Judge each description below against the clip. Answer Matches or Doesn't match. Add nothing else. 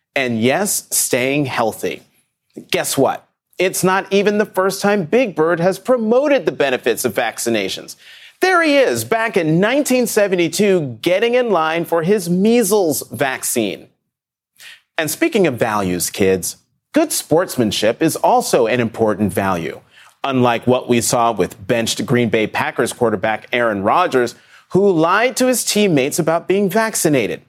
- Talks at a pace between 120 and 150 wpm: Matches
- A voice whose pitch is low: Doesn't match